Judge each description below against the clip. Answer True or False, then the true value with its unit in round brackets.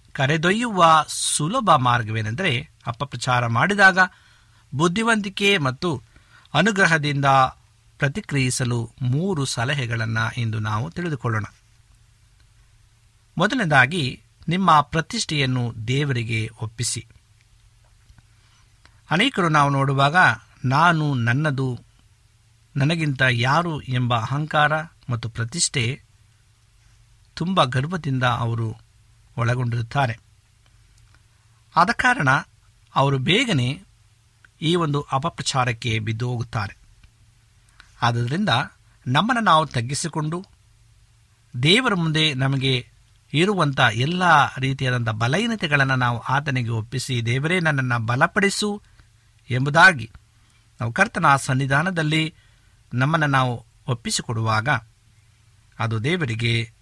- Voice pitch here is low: True (125 Hz)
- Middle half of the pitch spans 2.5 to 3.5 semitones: False (5.0 semitones)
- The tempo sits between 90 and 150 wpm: False (75 wpm)